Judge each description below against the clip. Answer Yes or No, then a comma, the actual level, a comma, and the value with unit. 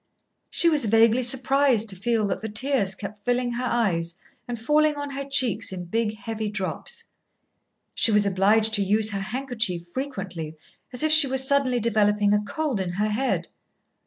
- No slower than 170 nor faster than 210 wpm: Yes, average, 175 wpm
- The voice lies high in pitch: Yes, high, 225 Hz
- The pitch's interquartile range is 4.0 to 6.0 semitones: Yes, average, 4.3 semitones